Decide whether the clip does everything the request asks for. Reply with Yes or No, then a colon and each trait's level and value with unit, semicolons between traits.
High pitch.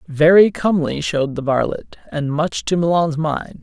No: medium, 160 Hz